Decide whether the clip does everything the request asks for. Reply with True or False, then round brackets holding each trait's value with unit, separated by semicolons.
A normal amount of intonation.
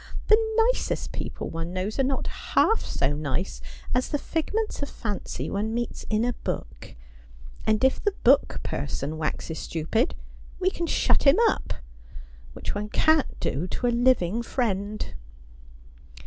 False (8.5 semitones)